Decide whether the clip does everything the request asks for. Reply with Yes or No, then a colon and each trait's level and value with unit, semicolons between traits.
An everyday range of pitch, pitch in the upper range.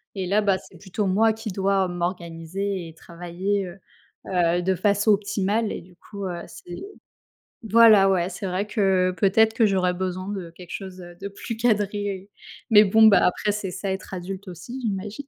No: narrow, 2.3 semitones; high, 195 Hz